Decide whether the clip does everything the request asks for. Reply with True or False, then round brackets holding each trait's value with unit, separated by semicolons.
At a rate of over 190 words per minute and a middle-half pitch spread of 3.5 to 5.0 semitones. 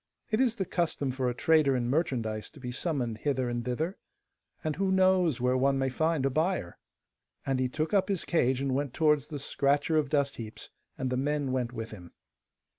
True (205 wpm; 4.0 semitones)